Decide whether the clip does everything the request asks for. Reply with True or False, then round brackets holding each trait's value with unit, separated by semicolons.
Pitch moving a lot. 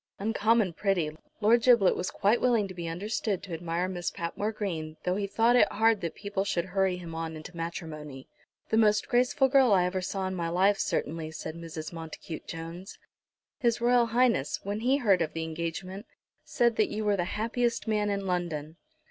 False (4.7 semitones)